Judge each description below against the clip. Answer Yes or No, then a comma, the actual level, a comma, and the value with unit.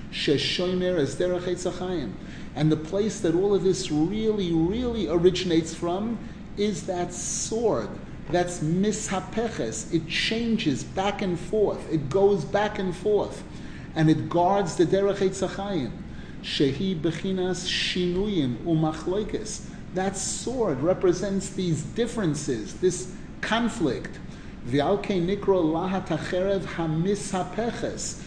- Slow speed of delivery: Yes, slow, 100 wpm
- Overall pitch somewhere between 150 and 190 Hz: Yes, medium, 185 Hz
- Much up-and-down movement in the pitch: No, average, 3.0 semitones